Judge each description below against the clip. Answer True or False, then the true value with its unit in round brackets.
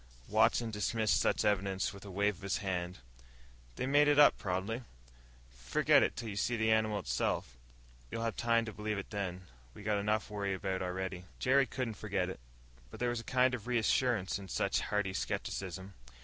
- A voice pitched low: True (105 Hz)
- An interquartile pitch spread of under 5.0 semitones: True (3.3 semitones)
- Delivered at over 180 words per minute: True (190 wpm)